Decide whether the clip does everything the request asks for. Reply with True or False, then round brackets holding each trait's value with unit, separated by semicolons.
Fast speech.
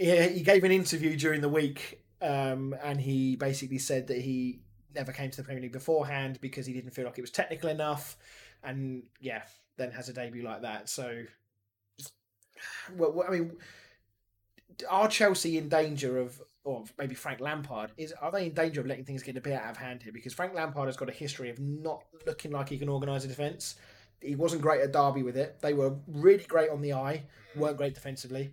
True (210 wpm)